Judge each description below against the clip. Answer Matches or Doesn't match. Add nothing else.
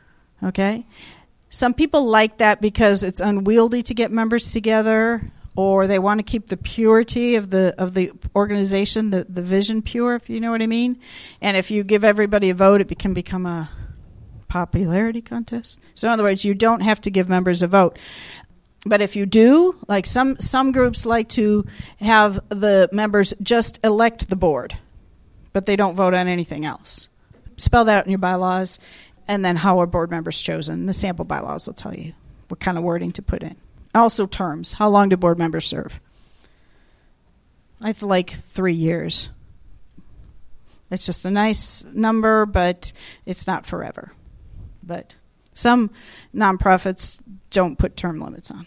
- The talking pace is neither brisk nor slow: Matches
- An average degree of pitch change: Matches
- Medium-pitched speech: Doesn't match